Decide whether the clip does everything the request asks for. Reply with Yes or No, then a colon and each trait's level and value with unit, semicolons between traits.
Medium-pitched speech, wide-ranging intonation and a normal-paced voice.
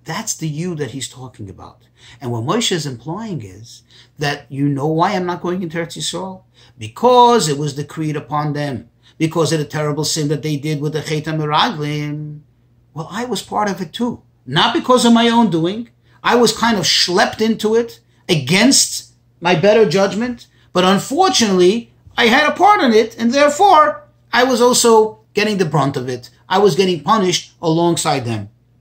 Yes: medium, 165 Hz; wide, 7.6 semitones; average, 185 wpm